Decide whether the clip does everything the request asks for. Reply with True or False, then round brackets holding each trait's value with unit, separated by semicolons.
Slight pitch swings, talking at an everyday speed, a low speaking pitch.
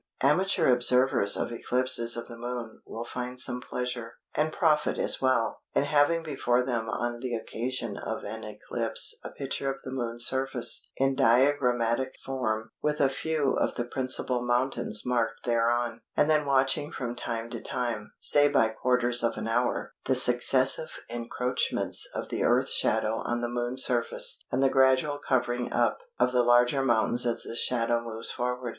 True (2.0 semitones; 170 wpm; 125 Hz)